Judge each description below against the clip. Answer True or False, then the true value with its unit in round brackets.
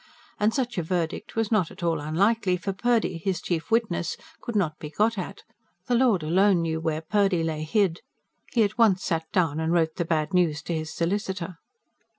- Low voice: False (180 Hz)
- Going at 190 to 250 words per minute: True (195 wpm)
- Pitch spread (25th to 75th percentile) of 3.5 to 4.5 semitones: True (4.2 semitones)